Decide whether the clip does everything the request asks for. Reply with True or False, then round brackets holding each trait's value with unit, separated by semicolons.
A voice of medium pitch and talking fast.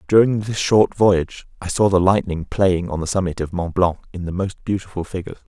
False (95 Hz; 215 wpm)